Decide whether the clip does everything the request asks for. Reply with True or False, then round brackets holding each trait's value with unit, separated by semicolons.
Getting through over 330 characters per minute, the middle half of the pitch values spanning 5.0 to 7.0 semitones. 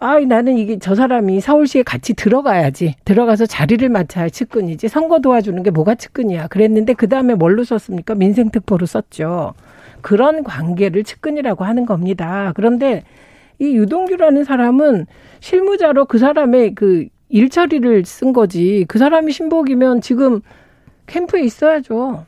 True (345 characters per minute; 5.5 semitones)